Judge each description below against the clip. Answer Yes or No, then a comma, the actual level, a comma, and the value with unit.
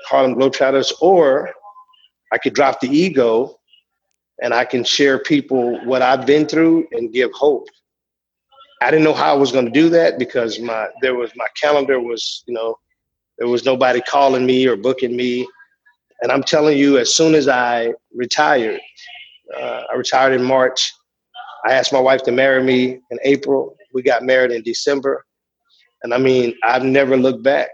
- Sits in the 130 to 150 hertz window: Yes, low, 135 Hz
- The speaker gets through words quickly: No, average, 175 wpm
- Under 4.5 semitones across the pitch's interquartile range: No, average, 4.8 semitones